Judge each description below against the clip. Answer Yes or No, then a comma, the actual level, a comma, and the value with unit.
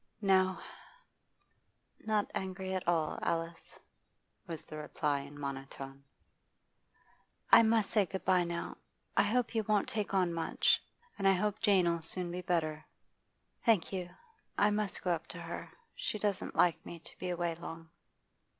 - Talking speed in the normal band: Yes, average, 160 wpm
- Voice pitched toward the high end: No, medium, 180 Hz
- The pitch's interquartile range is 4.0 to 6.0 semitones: No, average, 3.5 semitones